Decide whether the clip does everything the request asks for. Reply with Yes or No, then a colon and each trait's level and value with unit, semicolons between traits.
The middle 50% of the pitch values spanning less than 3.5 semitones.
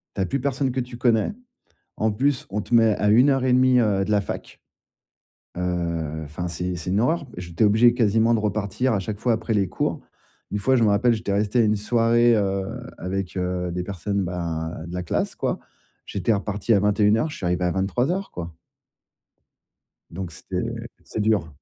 No: average, 4.6 semitones